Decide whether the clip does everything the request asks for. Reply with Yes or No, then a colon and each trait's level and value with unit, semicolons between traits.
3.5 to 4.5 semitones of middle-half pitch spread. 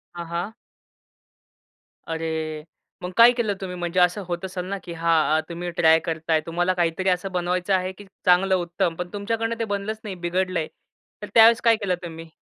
No: average, 2.9 semitones